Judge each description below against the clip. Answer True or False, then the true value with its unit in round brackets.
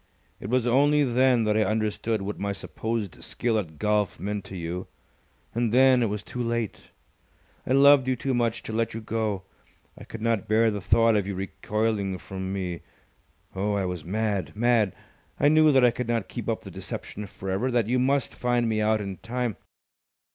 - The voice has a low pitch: True (110 Hz)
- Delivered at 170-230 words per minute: True (200 wpm)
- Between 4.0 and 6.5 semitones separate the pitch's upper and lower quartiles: False (3.3 semitones)